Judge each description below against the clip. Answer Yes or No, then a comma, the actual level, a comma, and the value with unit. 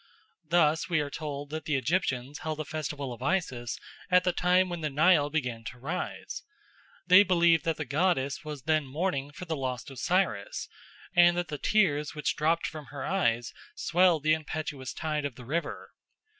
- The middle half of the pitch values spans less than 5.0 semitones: Yes, average, 3.8 semitones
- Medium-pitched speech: Yes, medium, 155 Hz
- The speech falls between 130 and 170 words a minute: No, average, 180 wpm